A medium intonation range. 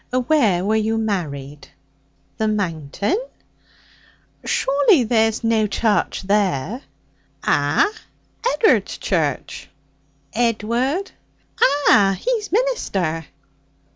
No: wide, 5.9 semitones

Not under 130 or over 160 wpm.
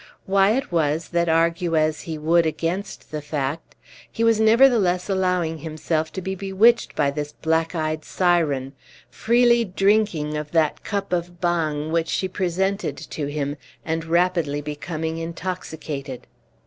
Yes: average, 145 wpm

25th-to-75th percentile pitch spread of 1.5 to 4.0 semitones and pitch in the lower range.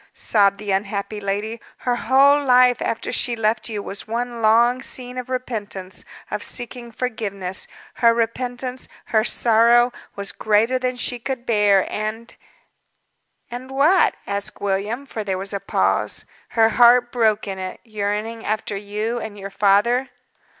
No: average, 3.3 semitones; high, 225 Hz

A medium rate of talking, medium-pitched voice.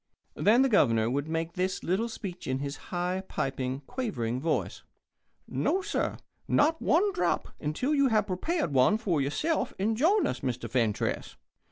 Yes: average, 160 wpm; medium, 180 Hz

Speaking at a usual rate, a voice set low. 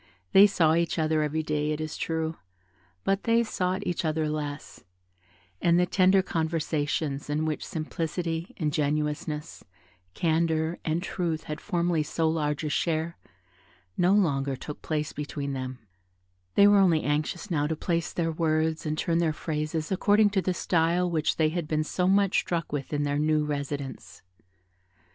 No: average, 160 wpm; medium, 160 Hz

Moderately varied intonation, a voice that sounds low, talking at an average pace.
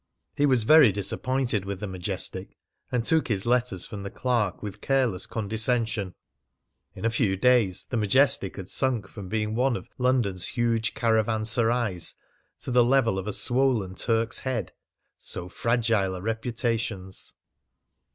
Yes: average, 3.8 semitones; low, 115 Hz; average, 145 wpm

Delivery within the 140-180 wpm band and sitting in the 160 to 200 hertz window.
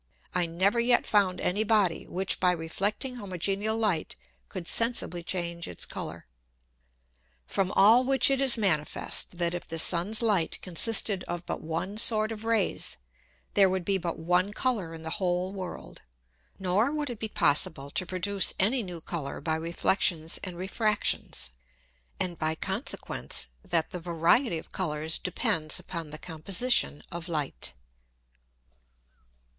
Yes: average, 145 wpm; medium, 185 Hz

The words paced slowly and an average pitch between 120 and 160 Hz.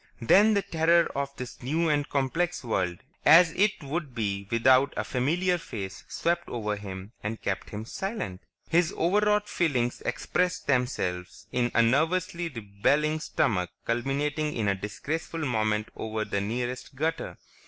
No: average, 145 wpm; low, 135 Hz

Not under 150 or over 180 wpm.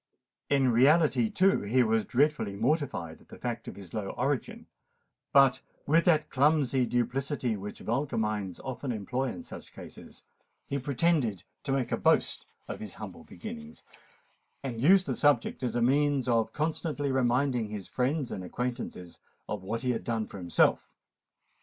Yes: average, 160 wpm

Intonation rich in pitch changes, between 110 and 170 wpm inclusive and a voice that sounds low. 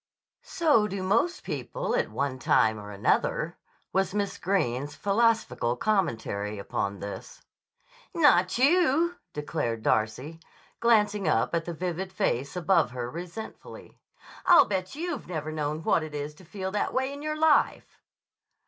No: wide, 8.1 semitones; average, 140 wpm; medium, 180 Hz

